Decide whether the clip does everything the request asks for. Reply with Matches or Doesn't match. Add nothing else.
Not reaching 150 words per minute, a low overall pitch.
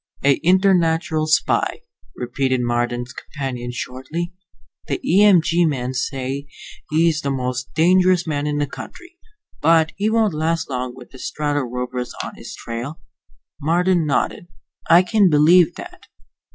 Doesn't match